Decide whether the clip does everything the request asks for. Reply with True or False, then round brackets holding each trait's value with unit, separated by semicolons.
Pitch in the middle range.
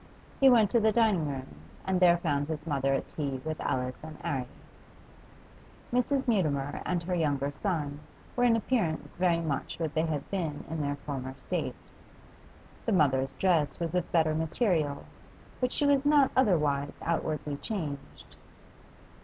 True (160 Hz)